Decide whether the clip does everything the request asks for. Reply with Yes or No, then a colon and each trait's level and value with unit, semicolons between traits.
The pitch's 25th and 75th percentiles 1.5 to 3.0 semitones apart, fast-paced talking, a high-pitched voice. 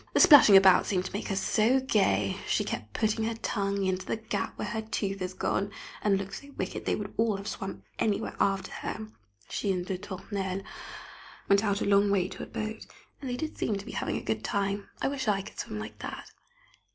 Yes: narrow, 2.4 semitones; fast, 225 wpm; high, 200 Hz